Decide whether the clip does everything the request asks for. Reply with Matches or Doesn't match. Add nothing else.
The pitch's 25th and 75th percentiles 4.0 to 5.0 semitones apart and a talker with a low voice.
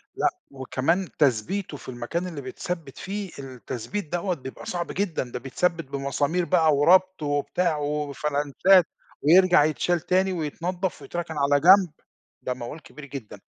Doesn't match